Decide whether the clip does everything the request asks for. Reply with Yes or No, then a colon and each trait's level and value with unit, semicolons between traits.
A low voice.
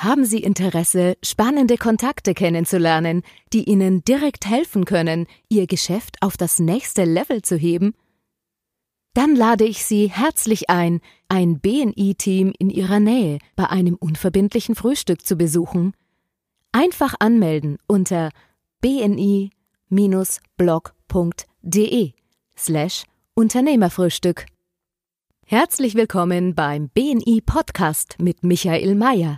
No: high, 190 Hz